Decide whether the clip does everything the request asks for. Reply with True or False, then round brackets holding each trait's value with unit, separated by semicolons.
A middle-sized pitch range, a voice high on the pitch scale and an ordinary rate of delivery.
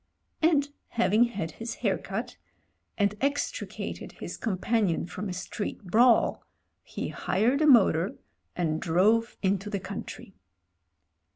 False (4.3 semitones; 210 Hz; 120 wpm)